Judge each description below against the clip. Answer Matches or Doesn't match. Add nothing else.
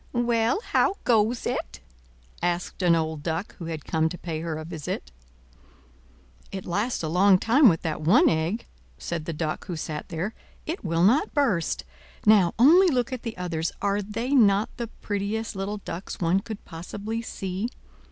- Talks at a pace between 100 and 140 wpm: Doesn't match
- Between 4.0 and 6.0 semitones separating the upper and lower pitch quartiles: Matches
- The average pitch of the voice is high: Matches